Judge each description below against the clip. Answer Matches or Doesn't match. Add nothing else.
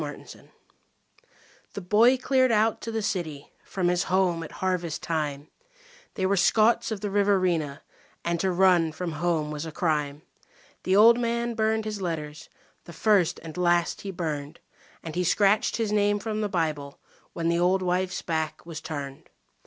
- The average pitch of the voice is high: Doesn't match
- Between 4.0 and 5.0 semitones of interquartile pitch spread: Matches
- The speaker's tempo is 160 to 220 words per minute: Matches